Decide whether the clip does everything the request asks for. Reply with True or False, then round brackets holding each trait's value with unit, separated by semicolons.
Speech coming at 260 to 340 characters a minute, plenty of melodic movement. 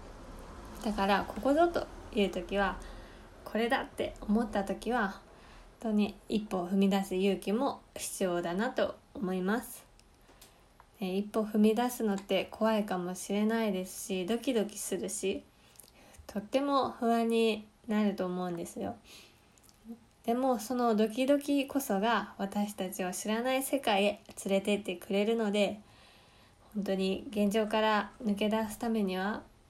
False (270 characters per minute; 2.9 semitones)